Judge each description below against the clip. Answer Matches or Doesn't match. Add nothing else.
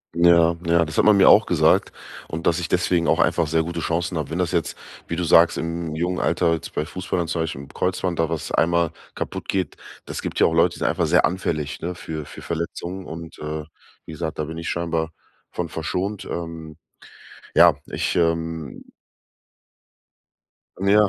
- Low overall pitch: Matches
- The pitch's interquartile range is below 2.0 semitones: Matches